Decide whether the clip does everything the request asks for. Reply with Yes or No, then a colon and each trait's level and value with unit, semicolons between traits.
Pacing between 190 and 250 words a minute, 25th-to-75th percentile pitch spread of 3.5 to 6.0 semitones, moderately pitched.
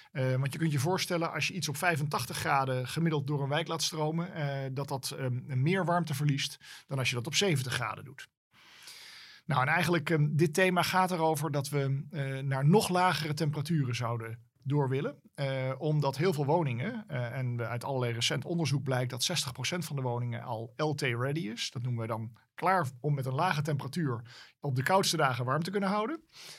Yes: fast, 200 wpm; average, 4.0 semitones; medium, 145 Hz